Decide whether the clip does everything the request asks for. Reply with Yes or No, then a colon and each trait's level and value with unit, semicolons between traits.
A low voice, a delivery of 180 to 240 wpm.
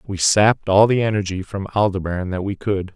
Yes: low, 100 Hz; fast, 205 wpm